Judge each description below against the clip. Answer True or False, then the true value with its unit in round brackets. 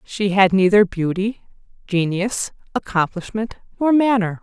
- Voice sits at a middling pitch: False (200 Hz)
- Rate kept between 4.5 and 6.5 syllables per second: False (4.2 syllables/s)